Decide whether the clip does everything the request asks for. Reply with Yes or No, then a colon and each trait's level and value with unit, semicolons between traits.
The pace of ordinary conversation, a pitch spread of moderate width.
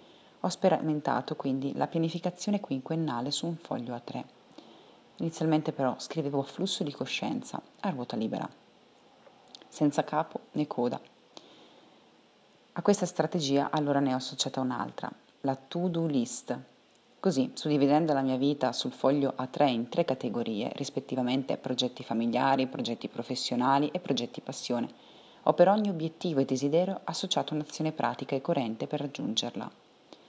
Yes: average, 135 wpm; average, 3.8 semitones